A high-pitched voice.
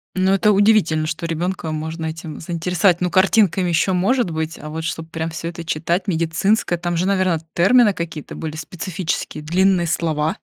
No: medium, 170 Hz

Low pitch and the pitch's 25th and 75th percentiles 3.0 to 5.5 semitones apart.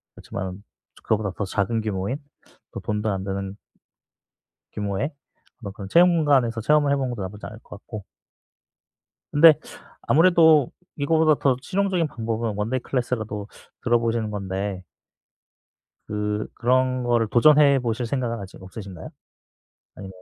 Yes: low, 115 Hz; average, 5.2 semitones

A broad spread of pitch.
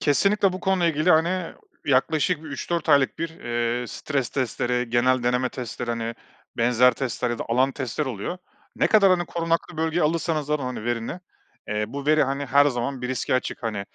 No: average, 4.8 semitones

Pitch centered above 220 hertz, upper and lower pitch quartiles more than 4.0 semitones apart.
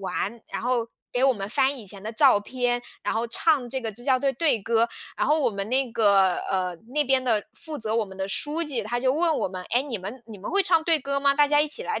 Yes: high, 245 Hz; average, 4.9 semitones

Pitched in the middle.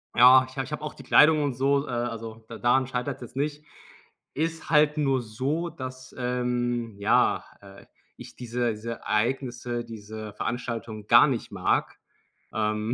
No: low, 125 Hz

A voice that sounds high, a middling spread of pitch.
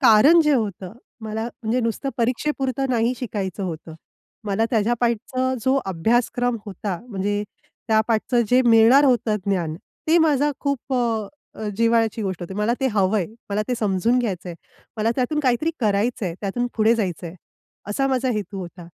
Yes: high, 225 Hz; average, 3.9 semitones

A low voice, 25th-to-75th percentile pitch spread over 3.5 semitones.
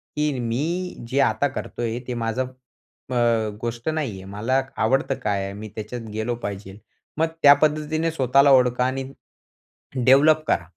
Yes: low, 125 Hz; average, 3.9 semitones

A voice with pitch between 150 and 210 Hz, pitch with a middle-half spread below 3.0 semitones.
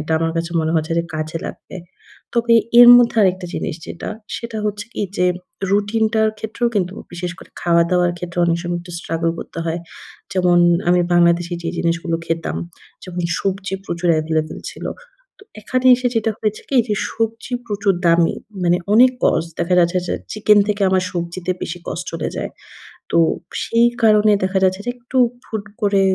No: medium, 185 Hz; average, 3.8 semitones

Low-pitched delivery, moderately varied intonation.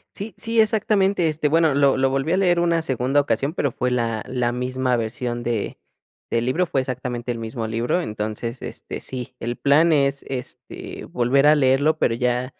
Yes: low, 130 Hz; average, 4.2 semitones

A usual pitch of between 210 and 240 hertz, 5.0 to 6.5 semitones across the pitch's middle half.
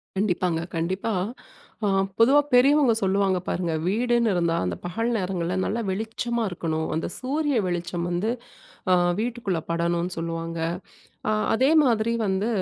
No: high, 190 Hz; average, 5.3 semitones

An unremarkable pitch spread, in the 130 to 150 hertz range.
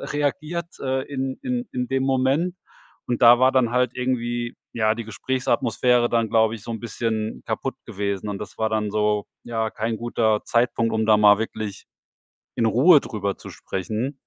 No: average, 3.1 semitones; low, 115 Hz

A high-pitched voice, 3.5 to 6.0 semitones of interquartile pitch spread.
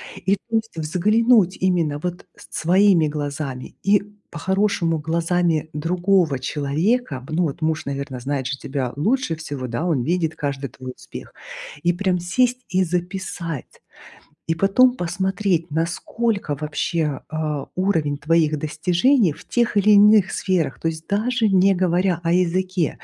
No: medium, 170 Hz; average, 4.1 semitones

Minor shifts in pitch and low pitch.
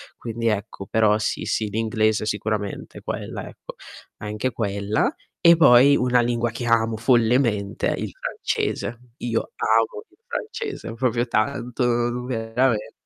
Yes: narrow, 2.2 semitones; low, 115 Hz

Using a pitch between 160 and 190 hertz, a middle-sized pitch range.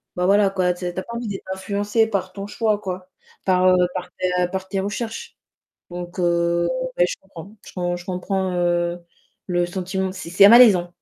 No: medium, 185 Hz; narrow, 2.1 semitones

